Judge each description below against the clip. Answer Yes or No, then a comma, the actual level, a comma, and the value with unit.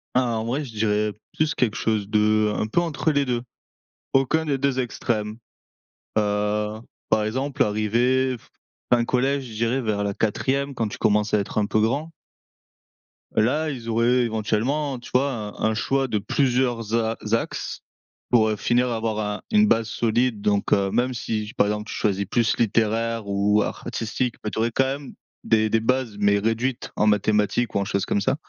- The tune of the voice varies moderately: Yes, average, 3.2 semitones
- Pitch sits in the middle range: No, low, 115 Hz